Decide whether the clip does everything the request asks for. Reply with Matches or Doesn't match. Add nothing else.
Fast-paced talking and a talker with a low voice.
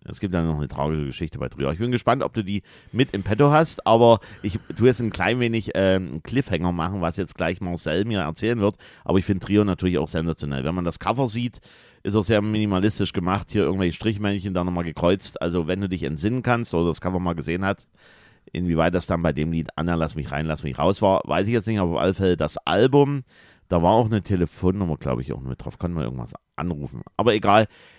Matches